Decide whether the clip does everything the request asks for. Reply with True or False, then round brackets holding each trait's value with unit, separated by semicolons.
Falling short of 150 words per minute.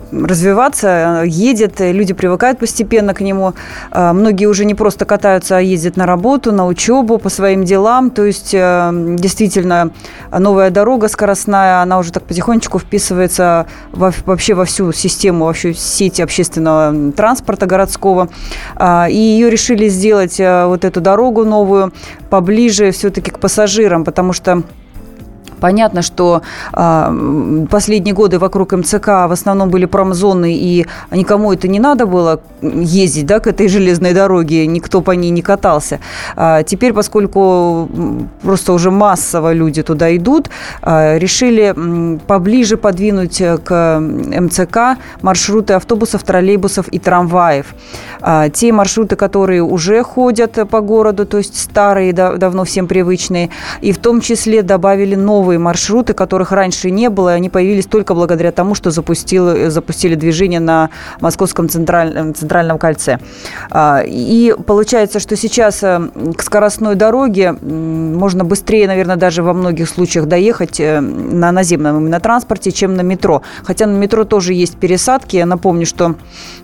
True (140 wpm)